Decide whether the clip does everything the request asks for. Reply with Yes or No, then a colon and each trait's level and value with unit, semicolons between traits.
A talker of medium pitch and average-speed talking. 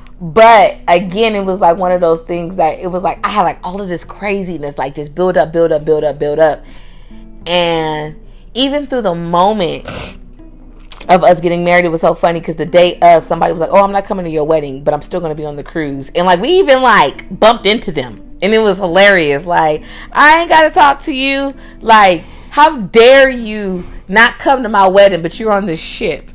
No: medium, 175 Hz; fast, 225 wpm